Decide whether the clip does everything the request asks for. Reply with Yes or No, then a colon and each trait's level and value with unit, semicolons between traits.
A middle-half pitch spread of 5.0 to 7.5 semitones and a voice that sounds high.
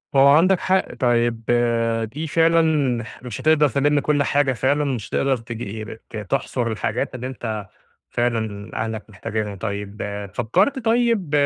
No: average, 5.3 semitones; low, 125 Hz